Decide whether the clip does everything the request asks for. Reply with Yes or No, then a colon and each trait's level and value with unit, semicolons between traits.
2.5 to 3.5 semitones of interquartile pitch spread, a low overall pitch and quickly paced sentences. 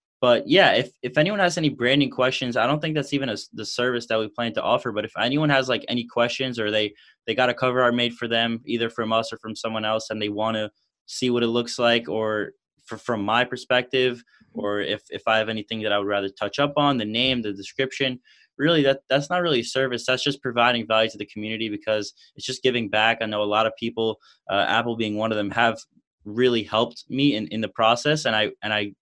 Yes: average, 2.8 semitones; low, 115 Hz; fast, 250 wpm